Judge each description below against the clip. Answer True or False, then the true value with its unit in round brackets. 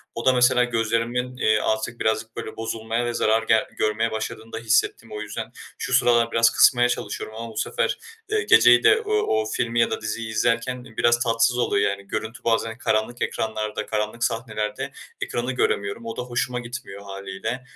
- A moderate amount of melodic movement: False (1.8 semitones)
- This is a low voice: True (115 Hz)